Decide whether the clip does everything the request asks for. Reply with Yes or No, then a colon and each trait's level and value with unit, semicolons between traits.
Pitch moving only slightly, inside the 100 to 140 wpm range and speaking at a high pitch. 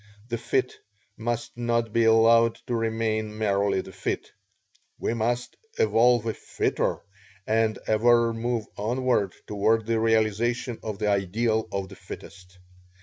No: narrow, 1.7 semitones; slow, 135 wpm; low, 115 Hz